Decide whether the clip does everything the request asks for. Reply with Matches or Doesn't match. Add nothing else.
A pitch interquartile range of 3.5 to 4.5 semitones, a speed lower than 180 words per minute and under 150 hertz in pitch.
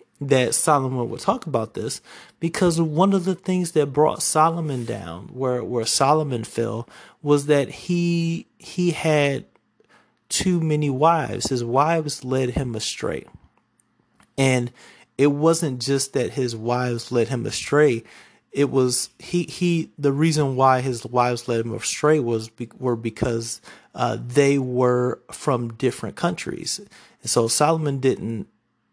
Matches